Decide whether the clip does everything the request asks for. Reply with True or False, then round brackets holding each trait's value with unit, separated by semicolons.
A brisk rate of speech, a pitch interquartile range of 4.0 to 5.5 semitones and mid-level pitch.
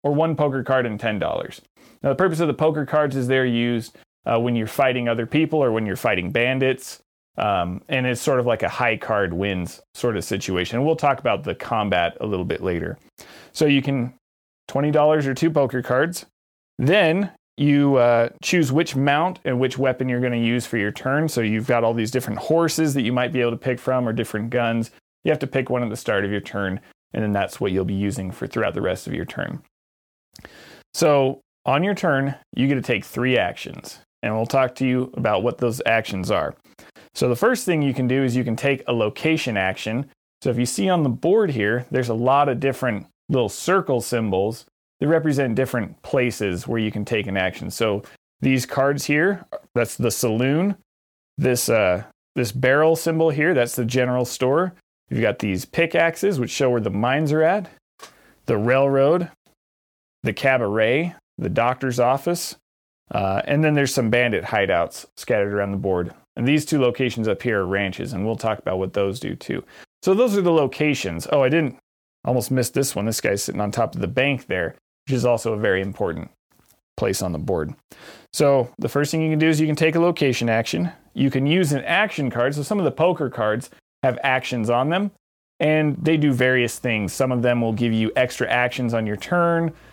False (210 wpm; 4.5 semitones; 125 Hz)